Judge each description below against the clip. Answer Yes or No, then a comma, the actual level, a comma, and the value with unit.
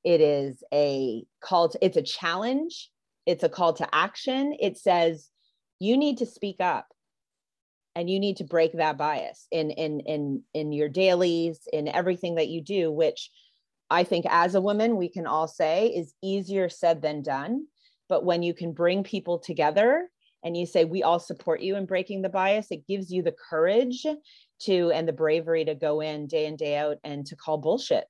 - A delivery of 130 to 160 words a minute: No, average, 195 wpm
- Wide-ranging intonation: No, average, 4.3 semitones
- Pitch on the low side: No, medium, 175 Hz